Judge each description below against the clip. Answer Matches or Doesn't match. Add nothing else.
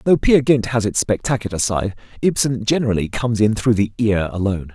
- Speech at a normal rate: Matches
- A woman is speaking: Doesn't match